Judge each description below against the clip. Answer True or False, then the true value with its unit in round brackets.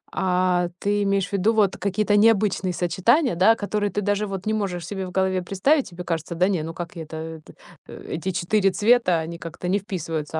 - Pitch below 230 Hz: True (190 Hz)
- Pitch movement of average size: True (3.0 semitones)